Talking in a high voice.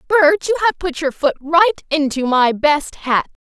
Yes: very high, 305 Hz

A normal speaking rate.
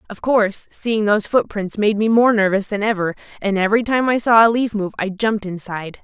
No: fast, 220 wpm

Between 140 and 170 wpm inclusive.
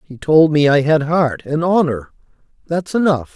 Yes: average, 160 wpm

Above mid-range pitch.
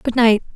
Yes: high, 230 Hz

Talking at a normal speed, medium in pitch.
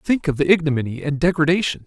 Yes: average, 195 wpm; medium, 155 Hz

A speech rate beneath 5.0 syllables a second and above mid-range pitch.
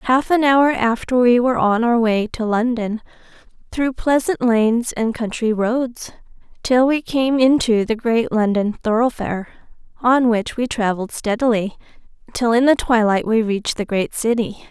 Yes: 4.8 syllables/s; high, 235 Hz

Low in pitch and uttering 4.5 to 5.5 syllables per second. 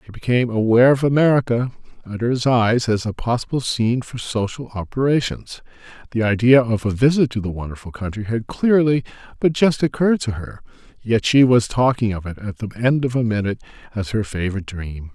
No: low, 115 Hz; 6.1 syllables/s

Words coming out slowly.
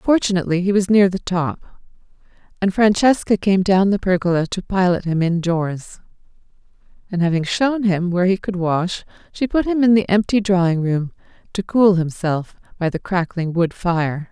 No: average, 170 wpm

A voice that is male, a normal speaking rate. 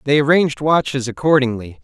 No: male; slow, 130 wpm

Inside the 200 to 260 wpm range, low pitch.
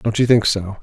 No: fast, 290 wpm; low, 110 Hz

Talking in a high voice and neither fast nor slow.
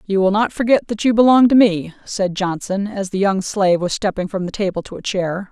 No: high, 200 Hz; fast, 250 wpm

